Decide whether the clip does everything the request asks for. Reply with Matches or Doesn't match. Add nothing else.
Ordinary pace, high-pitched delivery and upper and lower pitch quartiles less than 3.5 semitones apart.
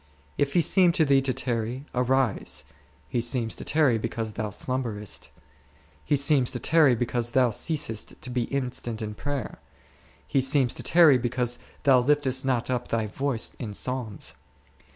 Doesn't match